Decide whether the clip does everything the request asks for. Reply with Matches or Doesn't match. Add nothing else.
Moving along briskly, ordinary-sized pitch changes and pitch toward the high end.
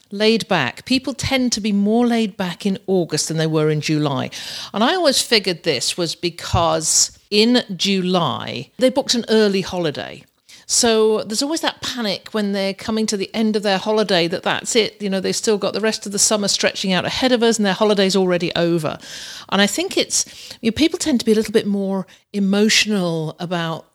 Matches